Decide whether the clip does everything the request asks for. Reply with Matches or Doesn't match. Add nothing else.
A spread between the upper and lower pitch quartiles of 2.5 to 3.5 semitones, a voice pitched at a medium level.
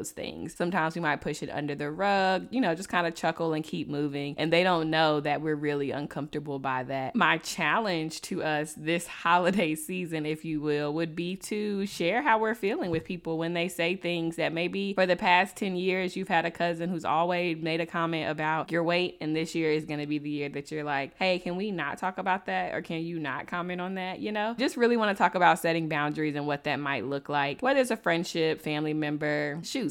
Matches